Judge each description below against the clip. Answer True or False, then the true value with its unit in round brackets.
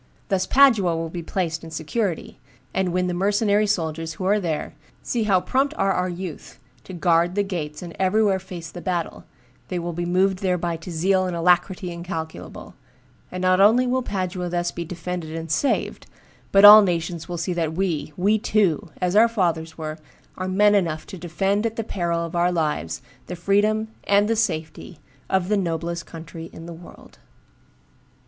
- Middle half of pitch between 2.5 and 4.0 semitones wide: True (2.9 semitones)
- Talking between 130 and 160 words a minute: False (185 wpm)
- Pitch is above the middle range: False (180 Hz)